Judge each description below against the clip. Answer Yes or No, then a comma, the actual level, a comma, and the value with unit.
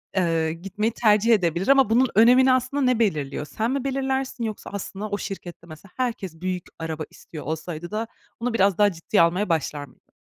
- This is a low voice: No, high, 200 Hz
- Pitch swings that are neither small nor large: No, wide, 5.9 semitones